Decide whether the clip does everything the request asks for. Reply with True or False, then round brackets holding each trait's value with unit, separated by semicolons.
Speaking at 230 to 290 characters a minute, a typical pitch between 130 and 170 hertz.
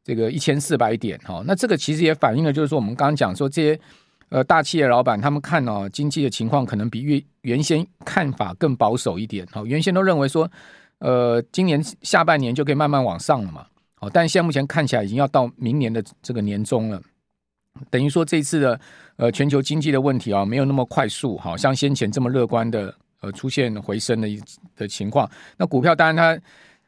False (320 characters per minute; 135 Hz)